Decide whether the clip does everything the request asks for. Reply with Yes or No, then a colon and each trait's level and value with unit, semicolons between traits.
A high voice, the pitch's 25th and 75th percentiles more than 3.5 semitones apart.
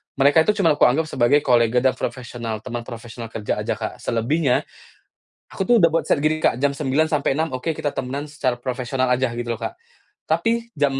No: low, 135 Hz; average, 4.1 semitones